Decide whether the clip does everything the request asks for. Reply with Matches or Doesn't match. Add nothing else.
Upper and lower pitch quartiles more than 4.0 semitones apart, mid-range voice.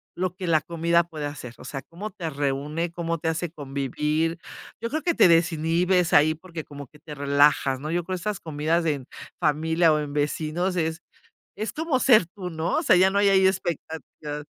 Doesn't match